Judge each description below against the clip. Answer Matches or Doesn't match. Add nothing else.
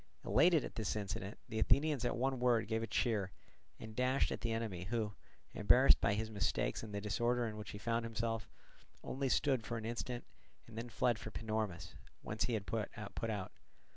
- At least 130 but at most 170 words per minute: Doesn't match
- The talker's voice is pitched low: Matches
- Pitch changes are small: Matches